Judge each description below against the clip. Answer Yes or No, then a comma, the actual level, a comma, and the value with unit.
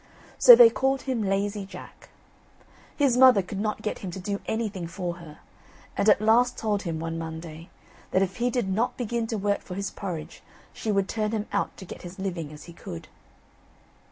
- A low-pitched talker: No, high, 200 Hz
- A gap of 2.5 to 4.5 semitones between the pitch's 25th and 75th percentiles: Yes, average, 4.0 semitones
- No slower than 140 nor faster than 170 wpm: No, average, 200 wpm